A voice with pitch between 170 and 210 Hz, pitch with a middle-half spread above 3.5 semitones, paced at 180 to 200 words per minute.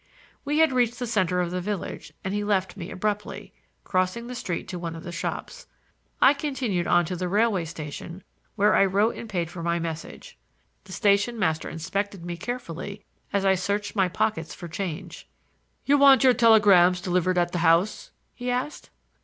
Yes: high, 190 Hz; average, 4.1 semitones; average, 185 wpm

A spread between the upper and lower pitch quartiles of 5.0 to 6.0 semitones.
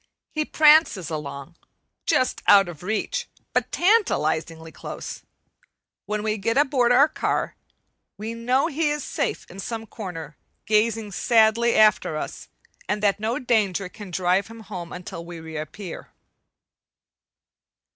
Yes: average, 5.3 semitones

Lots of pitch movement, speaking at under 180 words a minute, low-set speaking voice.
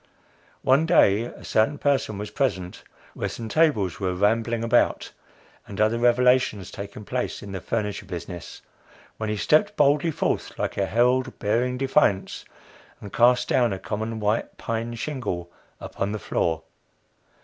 No: average, 3.8 semitones; average, 150 wpm; low, 115 Hz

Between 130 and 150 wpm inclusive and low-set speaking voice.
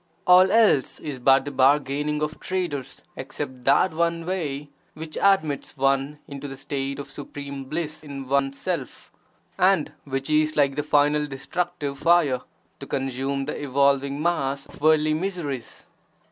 No: average, 145 wpm; medium, 145 Hz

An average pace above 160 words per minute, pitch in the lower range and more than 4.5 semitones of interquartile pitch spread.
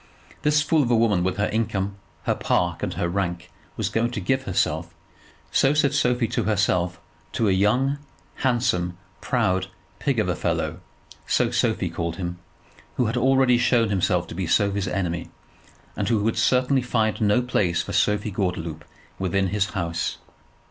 Yes: average, 170 wpm; low, 105 Hz; average, 5.1 semitones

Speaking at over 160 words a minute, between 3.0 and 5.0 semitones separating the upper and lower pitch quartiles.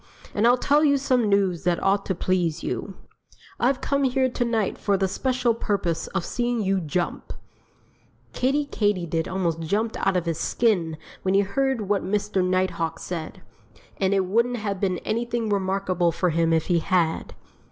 Yes: average, 175 wpm; average, 4.7 semitones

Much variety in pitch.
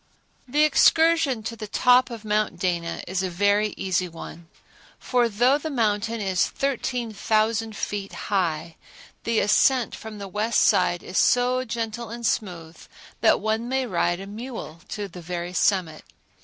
No: average, 4.4 semitones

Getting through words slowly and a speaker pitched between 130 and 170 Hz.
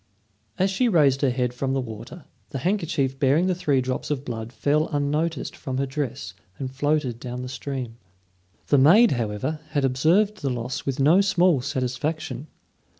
No: average, 170 wpm; low, 135 Hz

